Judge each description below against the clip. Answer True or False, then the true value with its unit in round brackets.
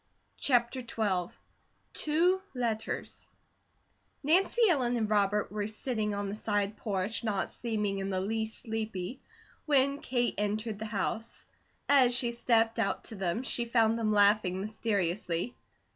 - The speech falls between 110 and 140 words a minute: True (135 wpm)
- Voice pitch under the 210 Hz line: False (220 Hz)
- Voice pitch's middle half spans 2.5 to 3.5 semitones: True (2.9 semitones)